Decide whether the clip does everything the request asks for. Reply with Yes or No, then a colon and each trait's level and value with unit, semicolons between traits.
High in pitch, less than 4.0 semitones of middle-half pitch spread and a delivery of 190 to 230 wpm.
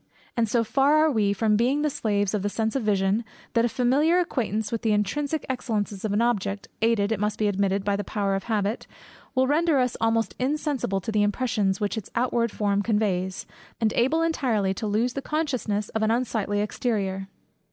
Yes: high, 220 Hz; average, 3.6 semitones; average, 200 wpm